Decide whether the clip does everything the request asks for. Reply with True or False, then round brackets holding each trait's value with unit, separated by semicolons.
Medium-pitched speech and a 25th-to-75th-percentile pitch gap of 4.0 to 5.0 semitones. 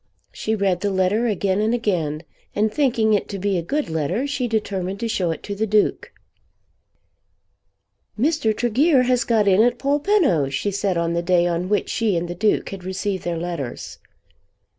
False (205 Hz; 4.5 semitones)